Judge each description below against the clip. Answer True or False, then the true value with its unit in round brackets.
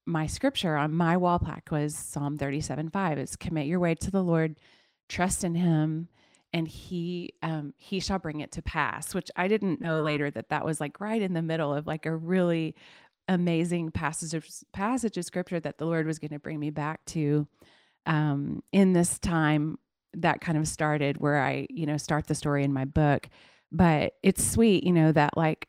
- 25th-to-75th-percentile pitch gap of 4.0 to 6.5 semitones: False (2.7 semitones)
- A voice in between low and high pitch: True (160 Hz)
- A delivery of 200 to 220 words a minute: True (205 wpm)